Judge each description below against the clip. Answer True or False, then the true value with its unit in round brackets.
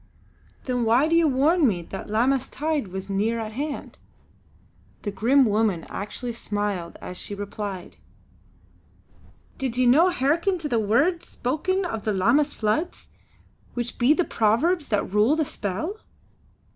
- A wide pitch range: True (6.4 semitones)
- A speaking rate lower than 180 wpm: True (150 wpm)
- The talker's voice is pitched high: True (240 Hz)